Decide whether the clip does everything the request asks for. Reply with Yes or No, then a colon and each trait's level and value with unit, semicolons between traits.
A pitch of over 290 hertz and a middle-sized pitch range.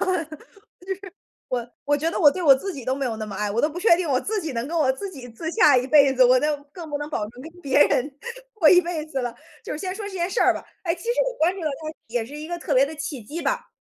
Yes: very high, 300 Hz; average, 4.9 semitones